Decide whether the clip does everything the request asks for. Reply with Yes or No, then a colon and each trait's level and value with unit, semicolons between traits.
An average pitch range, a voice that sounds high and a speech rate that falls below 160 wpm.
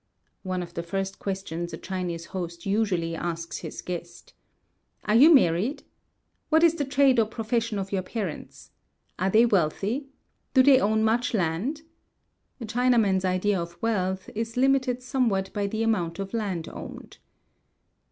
Yes: average, 4.7 semitones; high, 200 Hz; average, 150 wpm